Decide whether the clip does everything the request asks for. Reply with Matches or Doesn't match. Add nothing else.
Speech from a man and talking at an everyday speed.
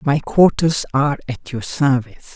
Doesn't match